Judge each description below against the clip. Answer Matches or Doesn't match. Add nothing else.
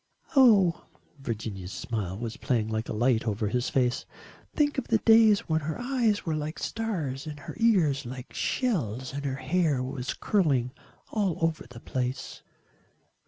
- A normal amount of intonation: Doesn't match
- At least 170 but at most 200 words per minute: Doesn't match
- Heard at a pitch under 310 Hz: Matches